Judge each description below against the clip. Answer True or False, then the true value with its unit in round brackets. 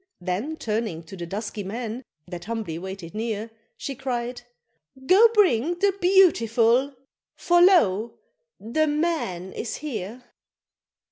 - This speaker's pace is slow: True (120 wpm)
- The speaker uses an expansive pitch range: True (7.6 semitones)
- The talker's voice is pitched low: False (230 Hz)